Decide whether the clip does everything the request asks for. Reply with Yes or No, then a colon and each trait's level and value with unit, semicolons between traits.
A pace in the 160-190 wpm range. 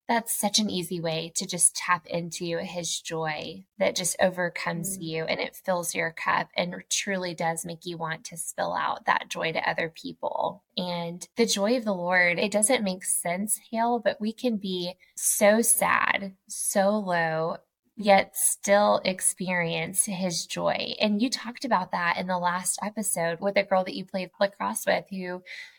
Yes: average, 175 wpm